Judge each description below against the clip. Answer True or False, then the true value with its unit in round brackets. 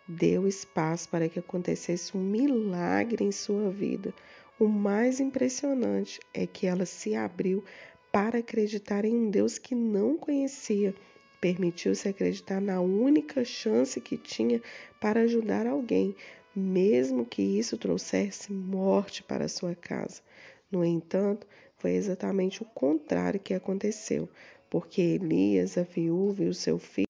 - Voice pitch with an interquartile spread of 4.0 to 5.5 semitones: True (4.3 semitones)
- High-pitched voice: True (195 Hz)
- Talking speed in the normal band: True (135 wpm)